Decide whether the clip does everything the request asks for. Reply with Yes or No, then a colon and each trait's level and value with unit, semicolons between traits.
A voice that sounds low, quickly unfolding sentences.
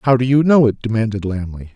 Yes: low, 115 Hz; fast, 240 wpm